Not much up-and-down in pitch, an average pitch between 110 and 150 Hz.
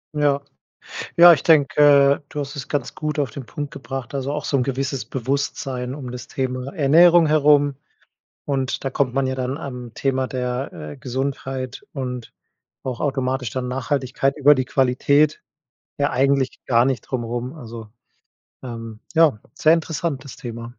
Yes: narrow, 2.3 semitones; low, 135 Hz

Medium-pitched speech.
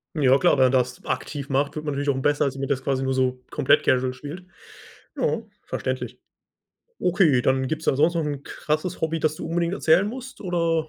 Yes: medium, 145 Hz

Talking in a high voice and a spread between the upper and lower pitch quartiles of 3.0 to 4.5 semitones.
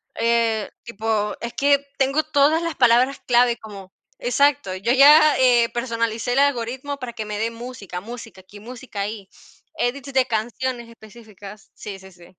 Yes: high, 235 Hz; average, 3.5 semitones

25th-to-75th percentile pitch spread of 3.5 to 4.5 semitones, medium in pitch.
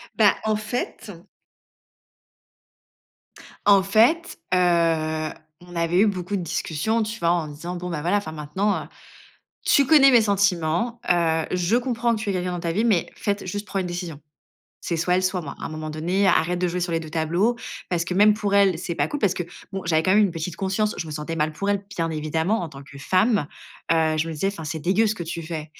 Yes: average, 3.9 semitones; medium, 180 Hz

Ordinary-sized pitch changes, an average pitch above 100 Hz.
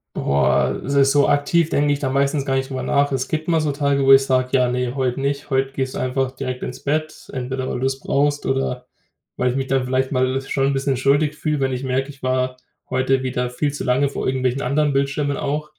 No: narrow, 1.6 semitones; low, 135 Hz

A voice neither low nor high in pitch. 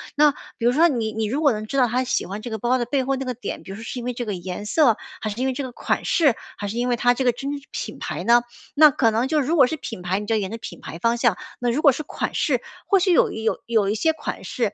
No: high, 240 Hz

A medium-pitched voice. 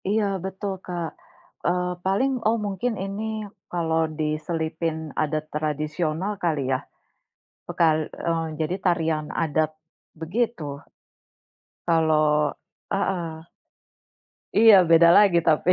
Yes: medium, 165 Hz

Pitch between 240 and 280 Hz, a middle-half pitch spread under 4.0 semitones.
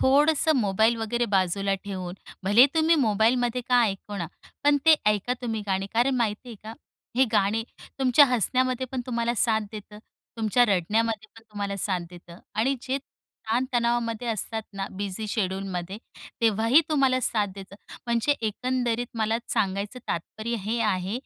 No: high, 225 Hz; average, 3.6 semitones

